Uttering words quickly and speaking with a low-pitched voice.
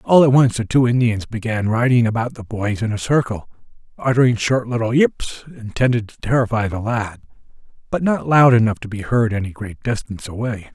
No: average, 190 wpm; low, 115 Hz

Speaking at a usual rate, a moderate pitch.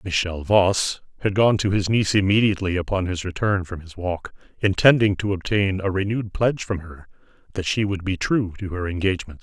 No: average, 190 wpm; very low, 95 Hz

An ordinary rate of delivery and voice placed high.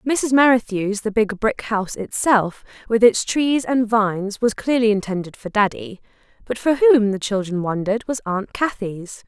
Yes: average, 170 wpm; high, 220 Hz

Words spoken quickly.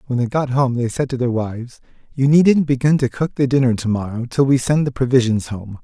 Yes: fast, 245 wpm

